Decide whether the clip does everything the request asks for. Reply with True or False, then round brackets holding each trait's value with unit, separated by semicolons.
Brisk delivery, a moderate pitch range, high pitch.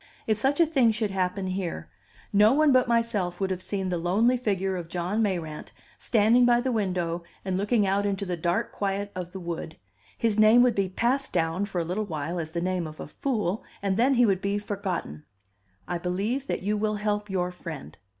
True (210 wpm; 3.5 semitones; 195 Hz)